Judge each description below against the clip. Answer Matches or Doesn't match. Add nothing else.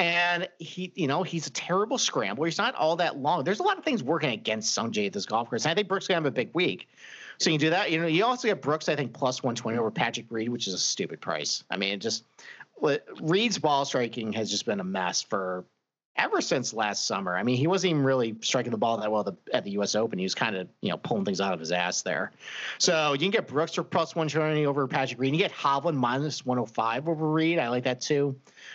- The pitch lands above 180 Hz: Doesn't match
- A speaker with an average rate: Doesn't match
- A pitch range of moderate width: Doesn't match